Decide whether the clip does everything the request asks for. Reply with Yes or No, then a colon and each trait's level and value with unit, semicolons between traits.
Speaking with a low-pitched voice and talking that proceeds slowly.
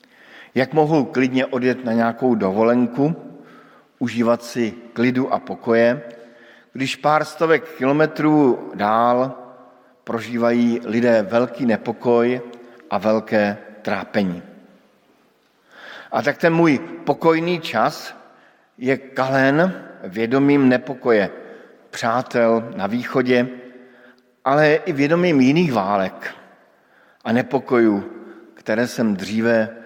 Yes: low, 125 Hz; slow, 95 wpm